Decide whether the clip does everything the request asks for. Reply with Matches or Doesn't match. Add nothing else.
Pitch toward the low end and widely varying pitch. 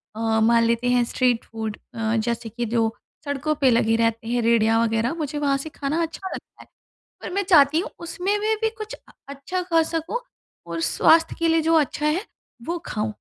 Doesn't match